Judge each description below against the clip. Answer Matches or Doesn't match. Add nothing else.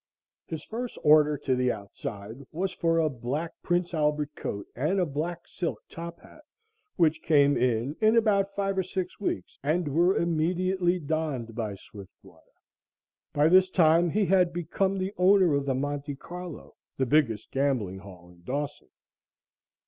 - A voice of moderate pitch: Matches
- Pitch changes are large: Doesn't match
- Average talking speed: Matches